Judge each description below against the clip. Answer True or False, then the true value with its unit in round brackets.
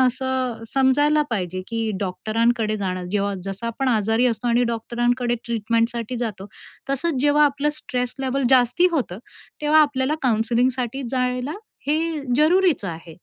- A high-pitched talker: True (245 Hz)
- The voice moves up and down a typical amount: True (3.3 semitones)